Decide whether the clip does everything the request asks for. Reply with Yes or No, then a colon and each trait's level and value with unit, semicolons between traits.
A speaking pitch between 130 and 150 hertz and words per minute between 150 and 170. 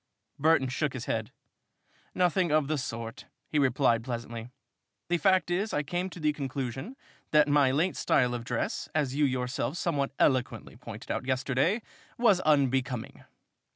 Yes: medium, 140 Hz; average, 155 wpm